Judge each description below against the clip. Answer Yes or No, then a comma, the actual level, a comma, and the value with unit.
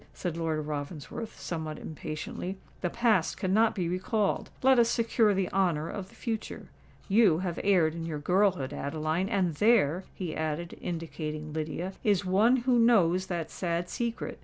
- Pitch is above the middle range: No, medium, 180 Hz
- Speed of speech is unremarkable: Yes, average, 160 wpm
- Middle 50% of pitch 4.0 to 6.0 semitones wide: Yes, average, 4.7 semitones